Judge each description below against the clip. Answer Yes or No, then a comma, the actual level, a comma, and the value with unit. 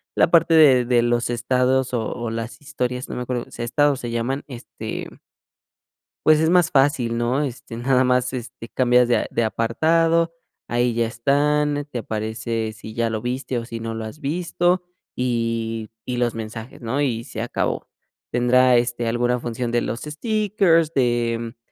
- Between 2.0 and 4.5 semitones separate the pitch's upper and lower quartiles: Yes, average, 3.2 semitones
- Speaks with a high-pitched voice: No, low, 125 Hz